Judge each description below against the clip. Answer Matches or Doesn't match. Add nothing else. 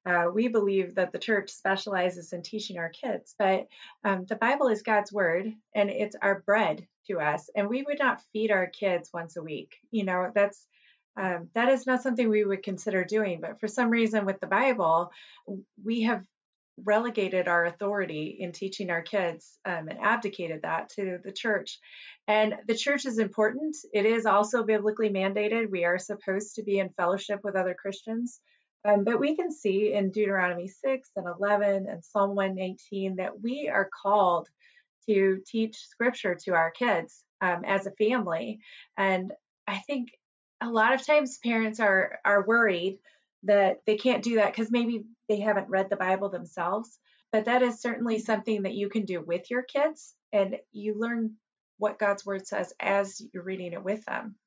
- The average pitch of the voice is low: Doesn't match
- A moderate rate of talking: Matches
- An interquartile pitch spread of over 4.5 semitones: Doesn't match